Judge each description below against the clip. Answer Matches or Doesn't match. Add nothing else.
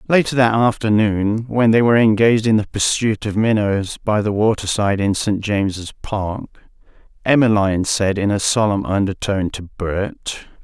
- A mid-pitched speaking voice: Doesn't match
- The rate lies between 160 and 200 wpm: Doesn't match